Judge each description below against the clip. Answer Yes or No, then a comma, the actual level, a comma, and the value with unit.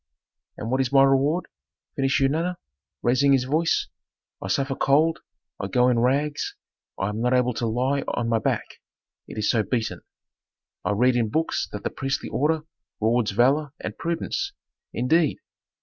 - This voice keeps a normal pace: Yes, average, 165 wpm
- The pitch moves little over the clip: No, average, 3.6 semitones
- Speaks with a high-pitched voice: No, low, 130 Hz